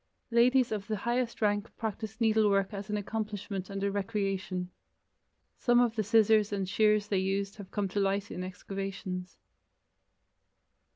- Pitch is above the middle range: Yes, high, 205 Hz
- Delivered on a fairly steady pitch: Yes, narrow, 2.0 semitones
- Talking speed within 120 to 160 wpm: Yes, average, 150 wpm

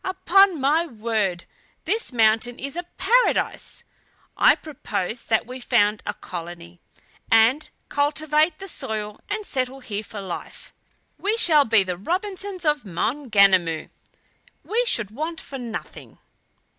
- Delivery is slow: Yes, slow, 130 wpm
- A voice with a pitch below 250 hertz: No, very high, 255 Hz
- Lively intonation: Yes, wide, 7.7 semitones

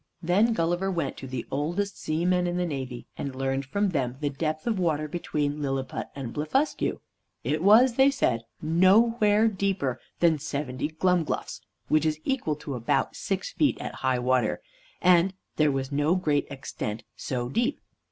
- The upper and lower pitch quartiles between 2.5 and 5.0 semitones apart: No, wide, 5.5 semitones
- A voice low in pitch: No, medium, 155 Hz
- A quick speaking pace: No, average, 160 wpm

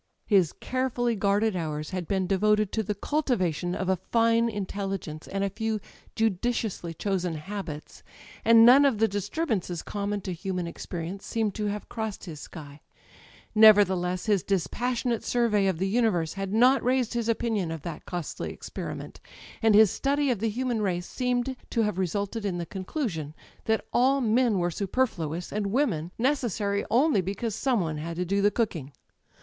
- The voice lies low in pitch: No, high, 205 Hz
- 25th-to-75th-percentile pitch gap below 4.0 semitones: No, average, 4.3 semitones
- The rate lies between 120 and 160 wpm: No, average, 170 wpm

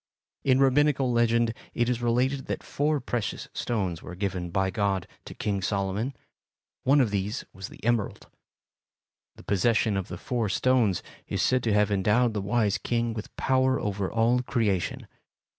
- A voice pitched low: Yes, low, 115 Hz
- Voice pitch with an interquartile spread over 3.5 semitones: Yes, average, 4.0 semitones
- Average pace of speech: Yes, average, 160 wpm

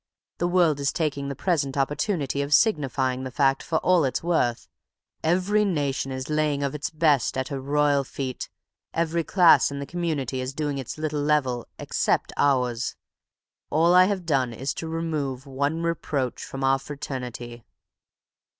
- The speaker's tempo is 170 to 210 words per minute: No, average, 160 wpm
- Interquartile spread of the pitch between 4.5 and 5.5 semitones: No, average, 3.4 semitones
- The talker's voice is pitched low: No, medium, 145 Hz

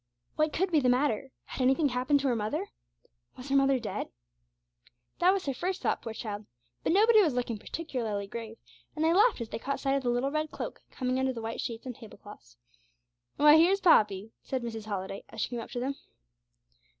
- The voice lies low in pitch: No, very high, 255 Hz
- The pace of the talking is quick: Yes, fast, 210 wpm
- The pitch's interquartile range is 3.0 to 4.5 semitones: No, average, 5.0 semitones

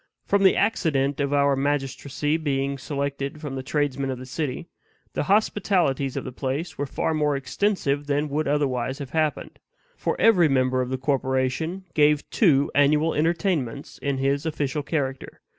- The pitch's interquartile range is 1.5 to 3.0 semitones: Yes, narrow, 2.5 semitones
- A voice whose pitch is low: No, medium, 145 Hz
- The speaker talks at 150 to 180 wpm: Yes, average, 160 wpm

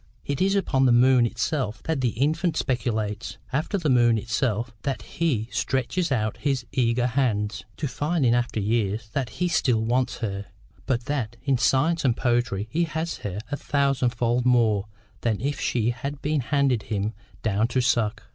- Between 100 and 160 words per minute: No, average, 170 wpm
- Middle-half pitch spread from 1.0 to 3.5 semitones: No, average, 3.9 semitones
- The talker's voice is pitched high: No, low, 120 Hz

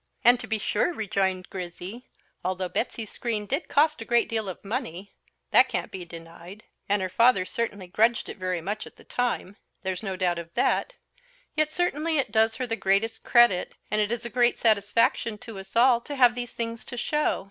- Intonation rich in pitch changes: No, average, 4.2 semitones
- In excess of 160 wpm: Yes, average, 200 wpm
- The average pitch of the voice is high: Yes, high, 220 Hz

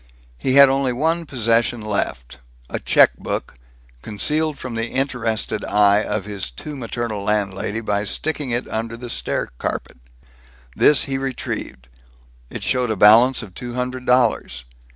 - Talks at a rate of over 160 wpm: No, average, 150 wpm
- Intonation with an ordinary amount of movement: Yes, average, 3.8 semitones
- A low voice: Yes, low, 115 Hz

